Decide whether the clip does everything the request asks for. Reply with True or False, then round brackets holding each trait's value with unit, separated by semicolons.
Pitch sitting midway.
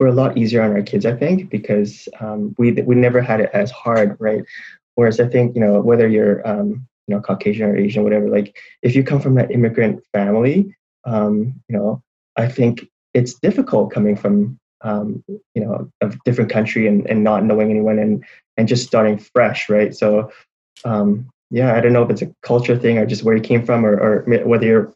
False (110 Hz)